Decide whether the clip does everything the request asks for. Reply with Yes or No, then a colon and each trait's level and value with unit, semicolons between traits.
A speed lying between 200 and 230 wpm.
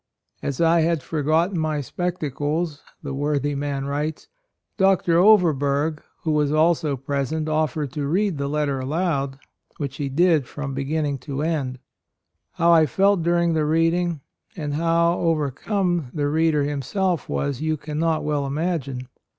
No: average, 160 wpm